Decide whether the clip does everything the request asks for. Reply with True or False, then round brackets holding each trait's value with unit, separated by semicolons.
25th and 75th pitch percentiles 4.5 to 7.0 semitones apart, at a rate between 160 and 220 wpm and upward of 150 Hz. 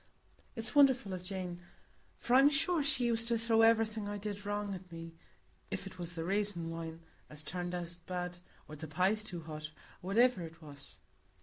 True (5.1 semitones; 185 wpm; 185 Hz)